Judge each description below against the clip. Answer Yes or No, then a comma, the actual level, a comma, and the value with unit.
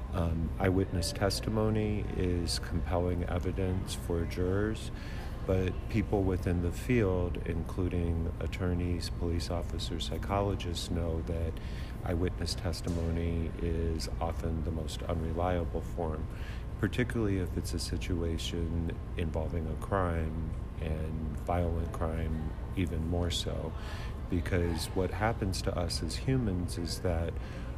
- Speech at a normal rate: No, slow, 110 wpm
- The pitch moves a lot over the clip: No, narrow, 2.5 semitones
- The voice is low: Yes, very low, 85 Hz